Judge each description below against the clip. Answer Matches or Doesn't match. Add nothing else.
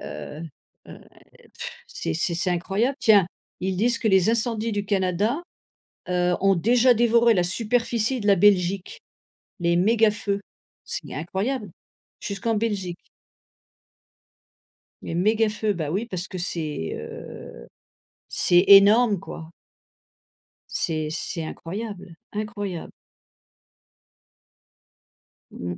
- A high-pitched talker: Matches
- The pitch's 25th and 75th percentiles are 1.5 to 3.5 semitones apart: Doesn't match